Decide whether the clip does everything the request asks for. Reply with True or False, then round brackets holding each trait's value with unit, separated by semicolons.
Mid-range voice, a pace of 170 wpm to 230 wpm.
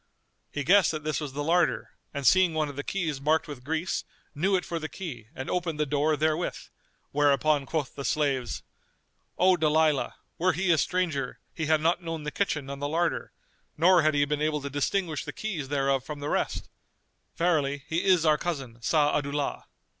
True (155 Hz; 190 wpm)